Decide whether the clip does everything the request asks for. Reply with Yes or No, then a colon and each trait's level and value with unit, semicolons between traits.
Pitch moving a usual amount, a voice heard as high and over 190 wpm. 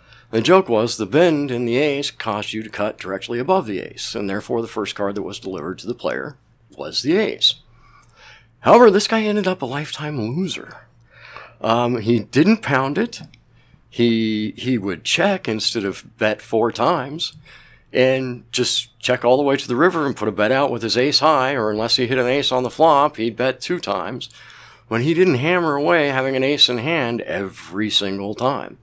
No: average, 4.2 semitones; low, 125 Hz; average, 200 wpm